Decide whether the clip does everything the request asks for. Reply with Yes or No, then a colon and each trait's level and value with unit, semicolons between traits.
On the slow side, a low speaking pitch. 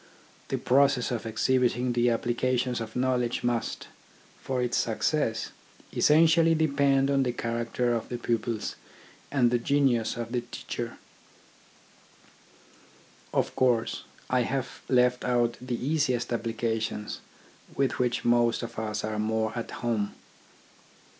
Yes: slow, 130 wpm; low, 120 Hz